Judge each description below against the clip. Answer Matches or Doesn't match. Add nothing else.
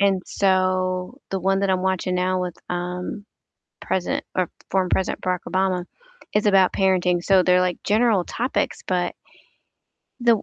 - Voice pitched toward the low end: Doesn't match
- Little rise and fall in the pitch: Matches